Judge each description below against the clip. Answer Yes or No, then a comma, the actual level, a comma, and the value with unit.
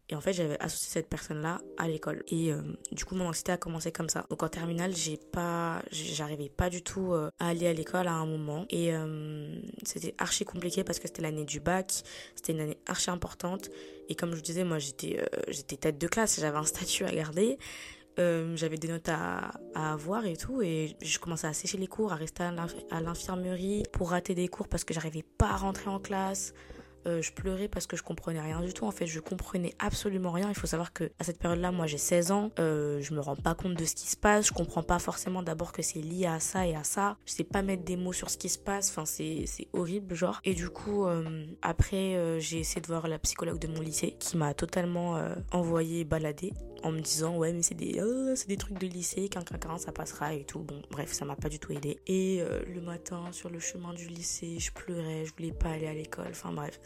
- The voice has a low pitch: No, medium, 170 Hz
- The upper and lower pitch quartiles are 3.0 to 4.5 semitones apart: No, narrow, 2.6 semitones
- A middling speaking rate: No, fast, 250 wpm